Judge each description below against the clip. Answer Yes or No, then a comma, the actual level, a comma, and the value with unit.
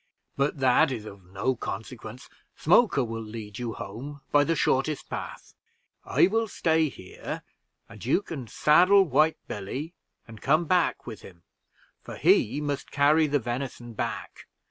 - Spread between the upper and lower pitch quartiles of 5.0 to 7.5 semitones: Yes, wide, 5.5 semitones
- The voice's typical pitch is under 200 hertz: Yes, low, 135 Hz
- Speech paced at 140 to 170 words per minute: Yes, average, 150 wpm